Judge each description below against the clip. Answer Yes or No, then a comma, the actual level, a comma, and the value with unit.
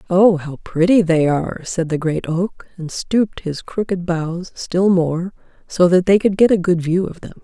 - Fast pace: Yes, fast, 210 wpm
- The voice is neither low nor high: Yes, medium, 175 Hz